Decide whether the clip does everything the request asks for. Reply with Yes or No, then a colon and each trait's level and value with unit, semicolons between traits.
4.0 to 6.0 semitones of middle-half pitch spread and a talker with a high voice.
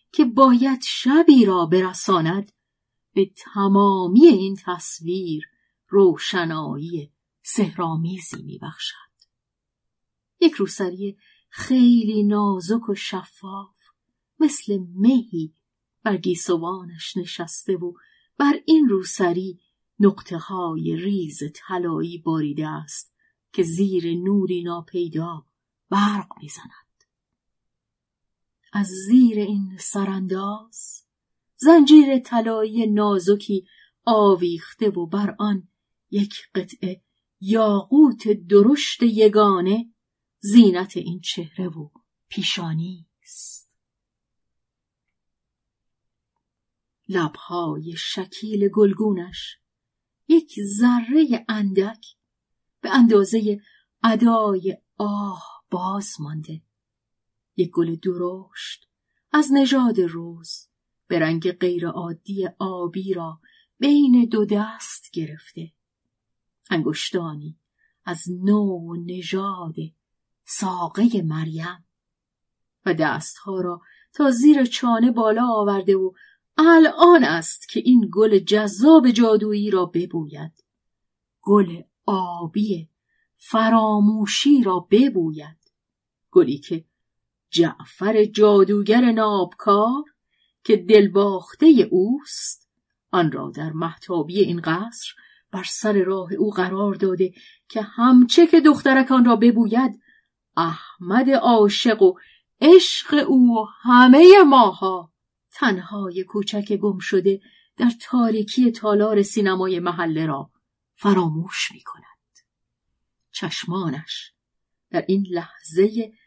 Yes: average, 4.4 semitones; high, 195 Hz